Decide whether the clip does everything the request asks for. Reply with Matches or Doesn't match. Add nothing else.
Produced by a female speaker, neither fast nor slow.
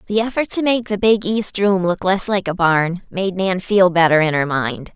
Doesn't match